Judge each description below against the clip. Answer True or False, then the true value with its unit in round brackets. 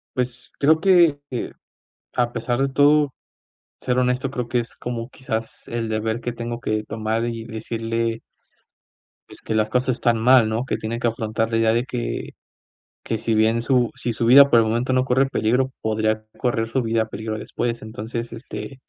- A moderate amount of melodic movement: False (2.0 semitones)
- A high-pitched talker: False (115 Hz)